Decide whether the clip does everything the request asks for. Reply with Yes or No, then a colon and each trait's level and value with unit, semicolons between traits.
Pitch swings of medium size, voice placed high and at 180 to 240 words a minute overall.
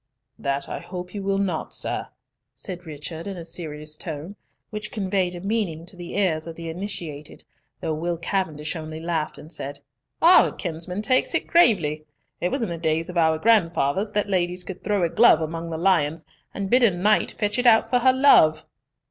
No: average, 4.1 semitones; medium, 175 Hz; average, 195 wpm